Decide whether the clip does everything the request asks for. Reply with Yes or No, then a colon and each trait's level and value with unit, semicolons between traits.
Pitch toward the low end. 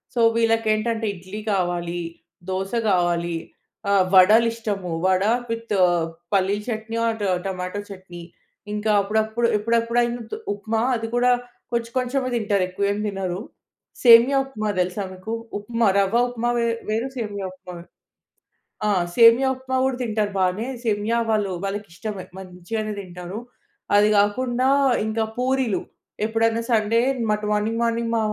No: high, 215 Hz